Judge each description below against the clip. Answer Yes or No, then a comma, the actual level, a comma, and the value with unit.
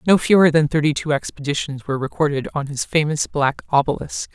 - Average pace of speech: Yes, average, 180 wpm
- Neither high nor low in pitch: Yes, medium, 150 Hz